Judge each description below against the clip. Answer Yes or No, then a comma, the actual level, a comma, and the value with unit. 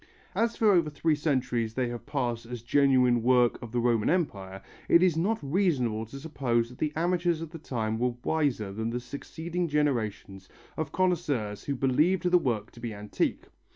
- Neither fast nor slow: Yes, average, 185 wpm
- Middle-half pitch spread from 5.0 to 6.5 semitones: Yes, wide, 5.6 semitones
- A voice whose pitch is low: Yes, low, 130 Hz